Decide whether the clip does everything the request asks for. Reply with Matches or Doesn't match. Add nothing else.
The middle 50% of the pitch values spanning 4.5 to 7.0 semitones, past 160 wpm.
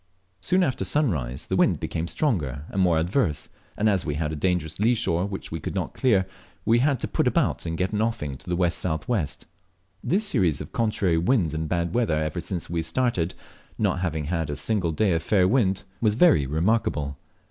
Matches